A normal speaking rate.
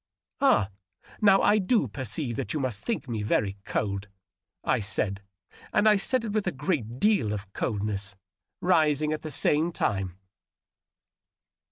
Yes: average, 155 wpm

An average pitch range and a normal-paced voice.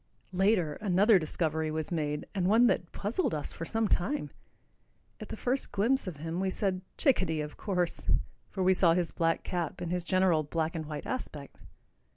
Yes: average, 3.8 semitones; average, 185 wpm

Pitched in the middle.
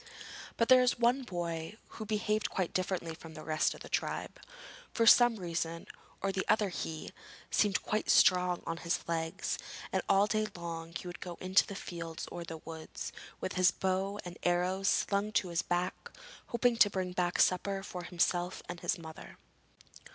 Yes: medium, 180 Hz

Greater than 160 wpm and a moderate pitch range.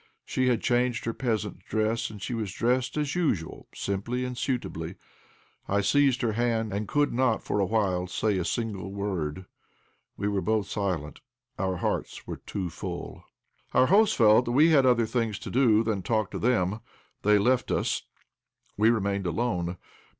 Yes: average, 170 wpm; average, 3.9 semitones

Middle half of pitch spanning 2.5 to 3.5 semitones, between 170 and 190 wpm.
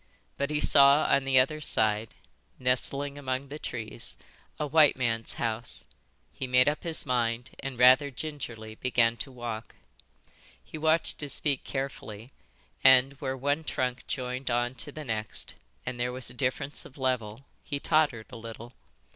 No: average, 3.0 semitones; average, 160 wpm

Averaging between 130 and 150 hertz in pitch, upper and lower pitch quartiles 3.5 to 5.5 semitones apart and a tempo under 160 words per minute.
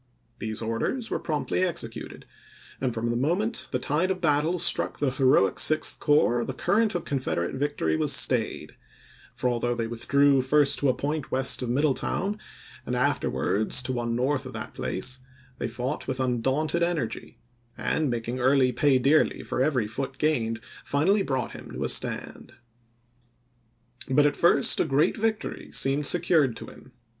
No: low, 135 Hz; average, 4.1 semitones; average, 165 wpm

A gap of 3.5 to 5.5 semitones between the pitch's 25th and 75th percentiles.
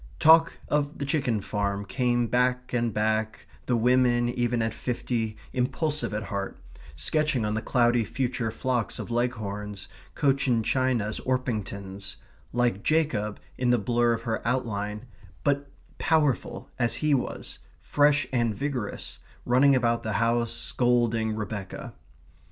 No: average, 2.9 semitones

